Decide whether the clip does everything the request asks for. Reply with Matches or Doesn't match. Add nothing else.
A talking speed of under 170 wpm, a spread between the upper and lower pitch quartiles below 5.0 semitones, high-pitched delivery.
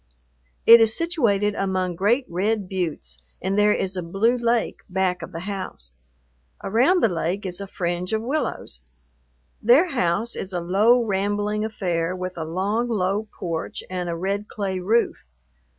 Matches